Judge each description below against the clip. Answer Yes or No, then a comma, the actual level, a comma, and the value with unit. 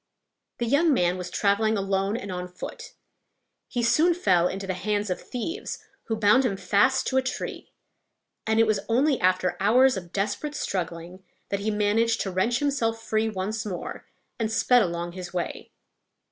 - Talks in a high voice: Yes, high, 210 Hz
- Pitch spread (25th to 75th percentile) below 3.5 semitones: No, average, 4.2 semitones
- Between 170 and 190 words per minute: Yes, average, 175 wpm